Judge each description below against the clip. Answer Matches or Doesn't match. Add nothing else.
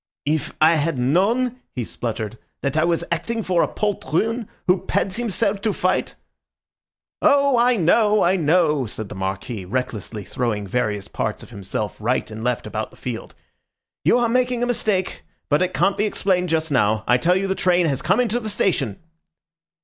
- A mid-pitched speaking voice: Matches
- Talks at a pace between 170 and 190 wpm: Matches